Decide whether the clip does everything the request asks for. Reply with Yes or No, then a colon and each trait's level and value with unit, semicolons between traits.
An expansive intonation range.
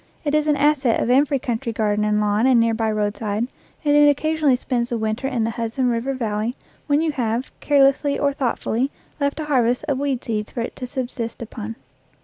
No: average, 3.9 semitones